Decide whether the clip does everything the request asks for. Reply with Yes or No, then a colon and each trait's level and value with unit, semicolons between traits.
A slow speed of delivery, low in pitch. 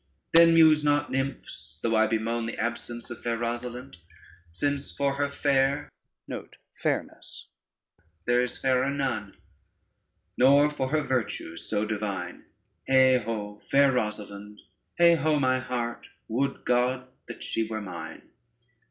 Yes: slow, 125 wpm; low, 125 Hz